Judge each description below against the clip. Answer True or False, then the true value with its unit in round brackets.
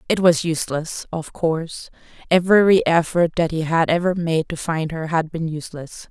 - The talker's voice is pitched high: False (165 Hz)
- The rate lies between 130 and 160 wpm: True (155 wpm)